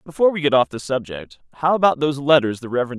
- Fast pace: Yes, fast, 240 wpm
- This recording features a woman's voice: No, male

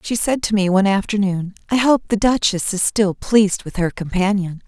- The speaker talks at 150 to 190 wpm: No, fast, 205 wpm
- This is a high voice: Yes, high, 200 Hz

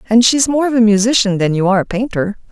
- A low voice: No, high, 220 Hz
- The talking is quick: Yes, fast, 260 wpm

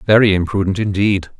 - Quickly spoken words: No, slow, 130 wpm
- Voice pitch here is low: Yes, low, 100 Hz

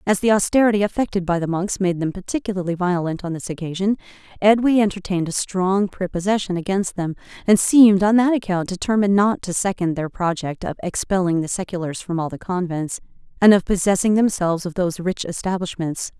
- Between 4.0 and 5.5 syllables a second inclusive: No, 5.9 syllables/s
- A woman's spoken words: Yes, female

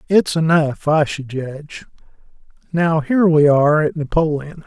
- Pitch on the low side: No, medium, 155 Hz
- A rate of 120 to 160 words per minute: Yes, average, 140 wpm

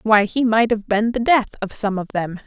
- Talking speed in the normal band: No, fast, 265 wpm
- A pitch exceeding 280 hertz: No, high, 215 Hz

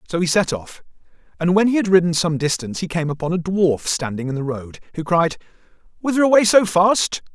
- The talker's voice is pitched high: No, medium, 170 Hz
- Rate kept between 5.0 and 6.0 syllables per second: Yes, 5.8 syllables/s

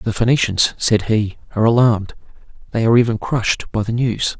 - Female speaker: No, male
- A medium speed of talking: Yes, average, 180 wpm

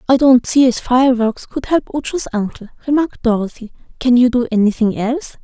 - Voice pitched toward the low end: No, very high, 250 Hz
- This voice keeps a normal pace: Yes, average, 175 wpm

